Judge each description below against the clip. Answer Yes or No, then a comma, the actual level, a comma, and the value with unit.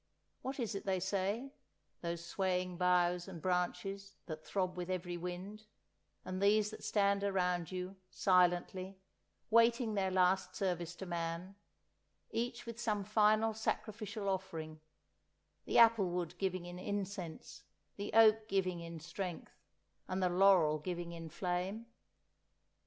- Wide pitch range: No, narrow, 2.5 semitones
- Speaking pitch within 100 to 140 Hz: No, medium, 185 Hz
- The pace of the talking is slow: Yes, slow, 130 wpm